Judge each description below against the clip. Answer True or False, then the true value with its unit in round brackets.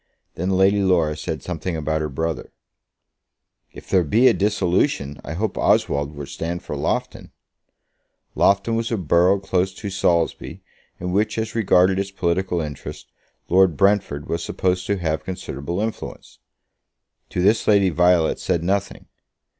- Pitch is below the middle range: True (90 Hz)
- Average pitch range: True (3.3 semitones)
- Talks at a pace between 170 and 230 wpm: False (145 wpm)